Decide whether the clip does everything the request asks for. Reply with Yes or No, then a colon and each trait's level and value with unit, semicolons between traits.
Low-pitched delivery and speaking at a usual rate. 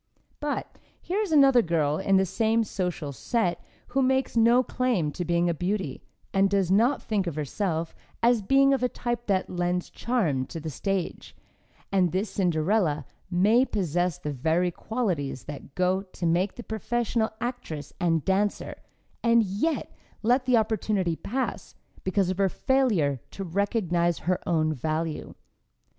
No: high, 190 Hz; average, 155 wpm